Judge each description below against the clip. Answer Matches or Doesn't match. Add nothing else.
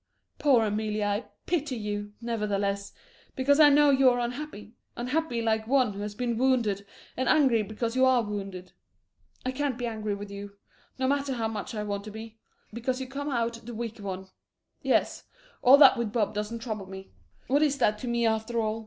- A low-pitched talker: Doesn't match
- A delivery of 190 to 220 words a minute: Matches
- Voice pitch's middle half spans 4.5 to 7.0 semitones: Doesn't match